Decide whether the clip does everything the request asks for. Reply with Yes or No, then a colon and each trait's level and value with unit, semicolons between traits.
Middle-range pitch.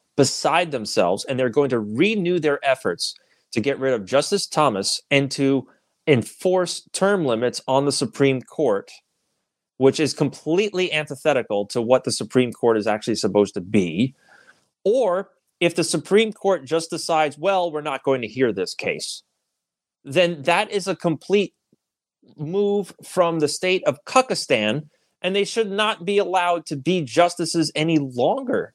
Yes: medium, 155 Hz